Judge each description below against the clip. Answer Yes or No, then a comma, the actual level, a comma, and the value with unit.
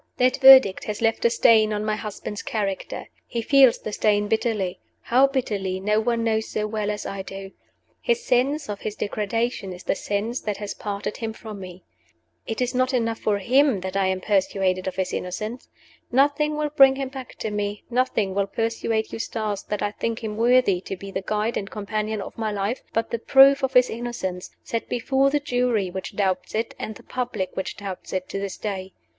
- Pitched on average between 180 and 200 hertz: No, high, 215 Hz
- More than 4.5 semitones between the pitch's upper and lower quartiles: No, average, 3.6 semitones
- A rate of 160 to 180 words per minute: No, fast, 205 wpm